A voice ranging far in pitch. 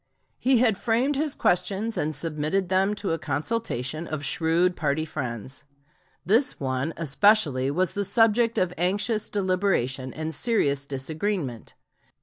Yes: wide, 6.6 semitones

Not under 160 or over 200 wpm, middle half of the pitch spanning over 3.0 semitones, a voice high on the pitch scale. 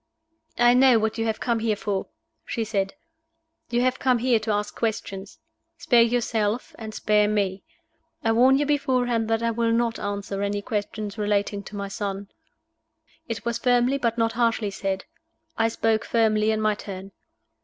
No: average, 170 wpm; narrow, 2.4 semitones; high, 220 Hz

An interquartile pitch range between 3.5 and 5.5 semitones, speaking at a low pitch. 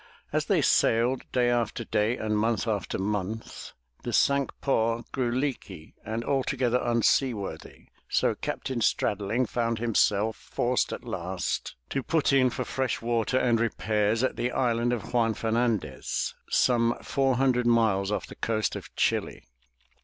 No: narrow, 2.5 semitones; low, 115 Hz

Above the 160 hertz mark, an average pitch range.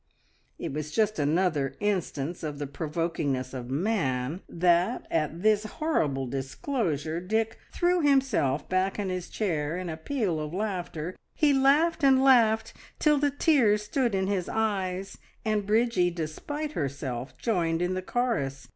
No: medium, 185 Hz; wide, 6.6 semitones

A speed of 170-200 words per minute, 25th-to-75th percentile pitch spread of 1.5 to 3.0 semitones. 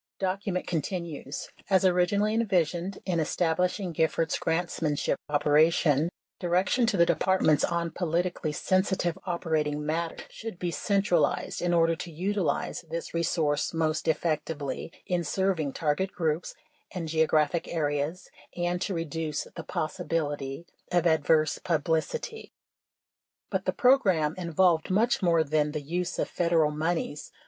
No: slow, 135 wpm; narrow, 2.6 semitones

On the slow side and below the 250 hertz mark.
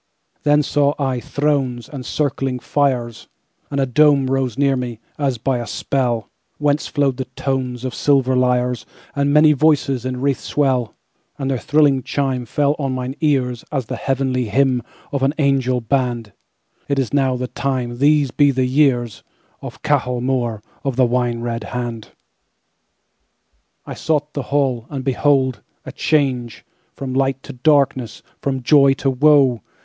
Yes: slow, 130 wpm; low, 135 Hz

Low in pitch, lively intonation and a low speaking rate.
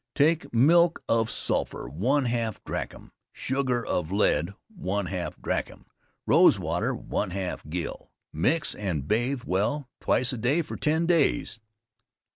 Yes: low, 120 Hz; wide, 7.2 semitones; slow, 120 wpm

